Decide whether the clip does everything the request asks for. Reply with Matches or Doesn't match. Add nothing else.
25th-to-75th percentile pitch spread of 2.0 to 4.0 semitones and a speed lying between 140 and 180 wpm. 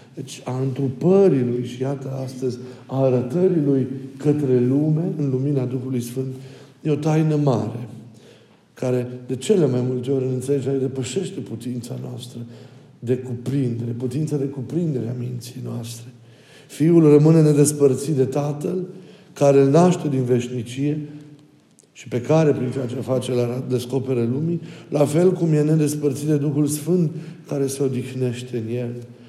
Matches